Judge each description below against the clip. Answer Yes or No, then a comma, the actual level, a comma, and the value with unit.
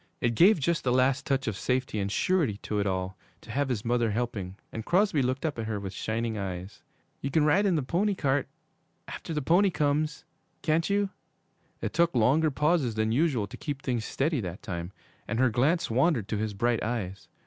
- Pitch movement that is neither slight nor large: No, wide, 6.0 semitones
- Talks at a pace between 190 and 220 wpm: Yes, fast, 205 wpm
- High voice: No, low, 125 Hz